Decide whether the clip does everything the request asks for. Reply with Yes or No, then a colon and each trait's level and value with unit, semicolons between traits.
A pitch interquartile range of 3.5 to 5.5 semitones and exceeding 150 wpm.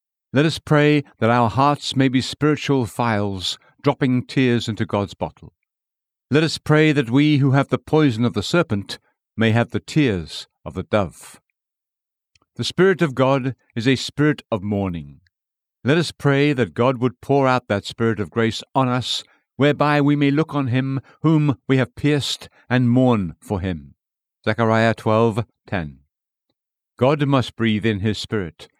Yes: average, 4.6 semitones; average, 165 wpm